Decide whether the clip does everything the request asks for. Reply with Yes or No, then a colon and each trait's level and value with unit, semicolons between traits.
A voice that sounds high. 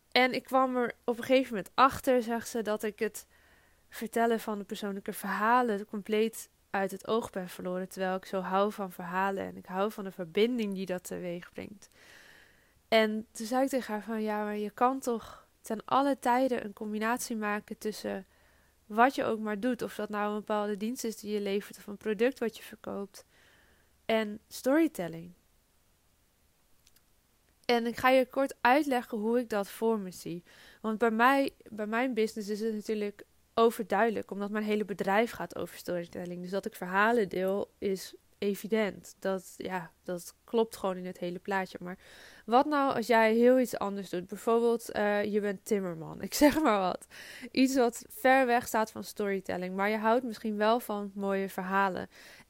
Yes: high, 215 Hz